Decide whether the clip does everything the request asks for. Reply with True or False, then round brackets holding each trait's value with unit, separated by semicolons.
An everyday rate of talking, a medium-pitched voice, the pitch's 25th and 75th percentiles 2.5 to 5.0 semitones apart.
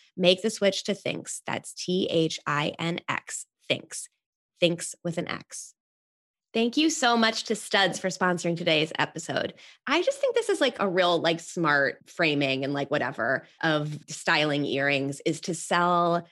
True (170 wpm; 175 Hz; 4.0 semitones)